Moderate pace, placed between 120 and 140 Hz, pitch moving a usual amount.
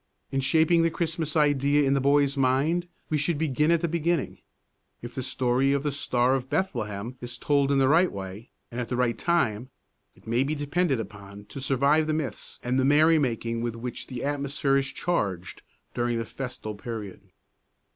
Yes: average, 190 wpm; low, 135 Hz; average, 4.0 semitones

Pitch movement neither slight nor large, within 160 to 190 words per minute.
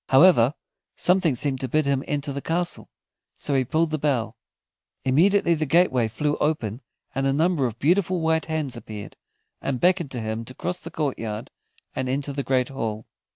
Yes: average, 4.1 semitones; average, 180 wpm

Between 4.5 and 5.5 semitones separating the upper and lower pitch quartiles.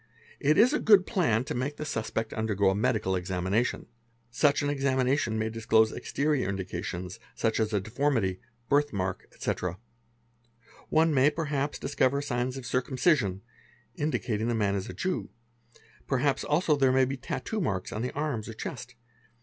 Yes: average, 5.2 semitones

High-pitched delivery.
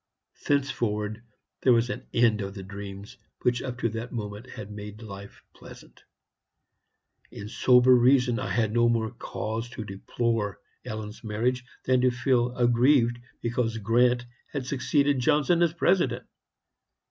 No: low, 120 Hz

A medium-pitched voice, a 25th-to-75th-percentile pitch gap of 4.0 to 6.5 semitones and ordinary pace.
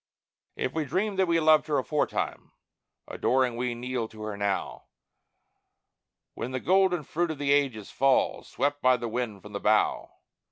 No: low, 130 Hz; average, 4.9 semitones; average, 165 wpm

